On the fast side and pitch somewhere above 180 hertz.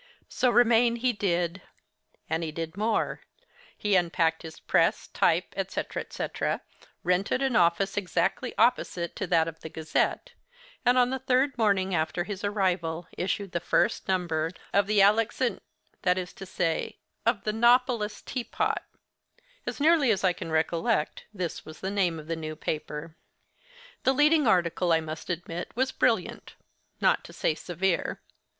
No: average, 150 wpm; high, 190 Hz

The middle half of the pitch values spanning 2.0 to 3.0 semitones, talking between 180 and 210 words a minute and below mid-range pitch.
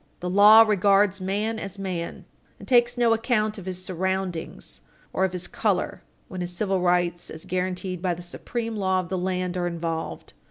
No: narrow, 2.5 semitones; average, 185 wpm; medium, 185 Hz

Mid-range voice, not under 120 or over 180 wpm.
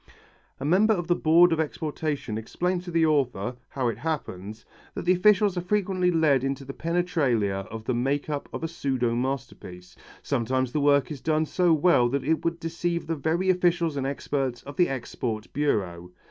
No: medium, 145 Hz; average, 190 wpm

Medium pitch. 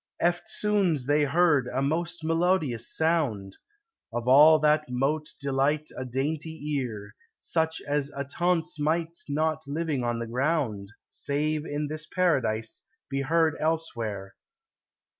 Yes: medium, 150 Hz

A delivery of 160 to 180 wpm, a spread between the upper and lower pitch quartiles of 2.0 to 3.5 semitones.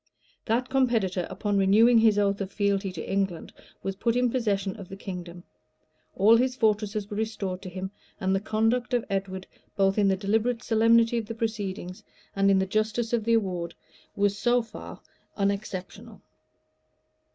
Yes: average, 165 wpm; average, 2.9 semitones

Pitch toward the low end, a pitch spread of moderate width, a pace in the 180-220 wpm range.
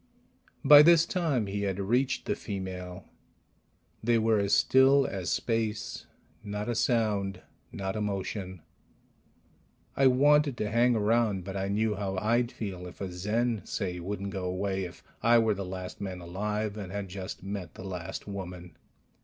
No: low, 100 Hz; average, 3.3 semitones; average, 160 wpm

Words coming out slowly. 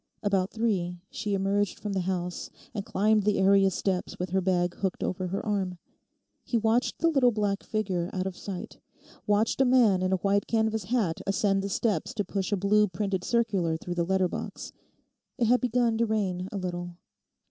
No: average, 190 wpm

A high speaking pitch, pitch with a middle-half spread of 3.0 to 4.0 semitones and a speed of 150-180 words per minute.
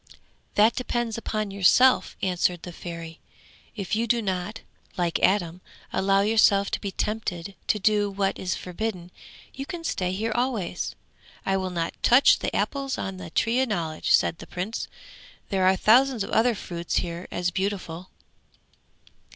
Yes: high, 195 Hz; average, 3.7 semitones; average, 160 wpm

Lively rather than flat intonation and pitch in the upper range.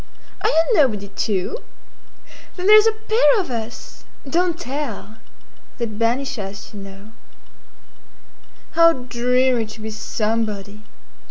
Yes: wide, 7.4 semitones; high, 235 Hz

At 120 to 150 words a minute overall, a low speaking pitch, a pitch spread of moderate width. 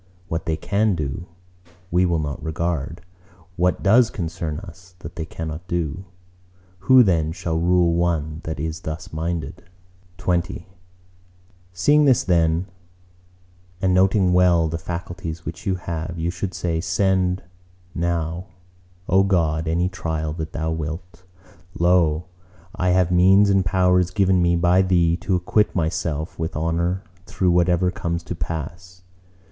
No: average, 140 wpm; very low, 85 Hz; narrow, 2.0 semitones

